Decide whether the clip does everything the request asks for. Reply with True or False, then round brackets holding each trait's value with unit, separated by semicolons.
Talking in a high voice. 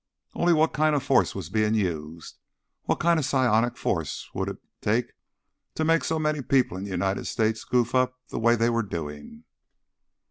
False (115 Hz)